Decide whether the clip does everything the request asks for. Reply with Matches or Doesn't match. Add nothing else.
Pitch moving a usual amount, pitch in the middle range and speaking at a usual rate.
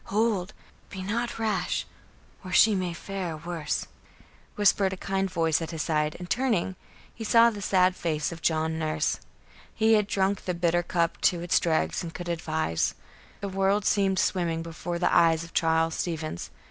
Matches